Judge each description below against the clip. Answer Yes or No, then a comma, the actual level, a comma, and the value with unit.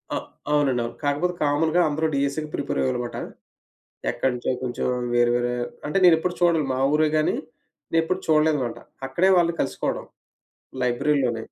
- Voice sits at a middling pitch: Yes, medium, 150 Hz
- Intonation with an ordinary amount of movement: Yes, average, 4.2 semitones